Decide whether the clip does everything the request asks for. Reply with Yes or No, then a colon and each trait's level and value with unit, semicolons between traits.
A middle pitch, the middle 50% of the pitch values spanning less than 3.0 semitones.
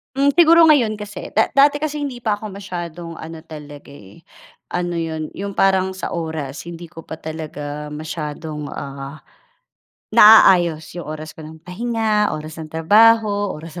No: medium, 170 Hz; average, 5.2 semitones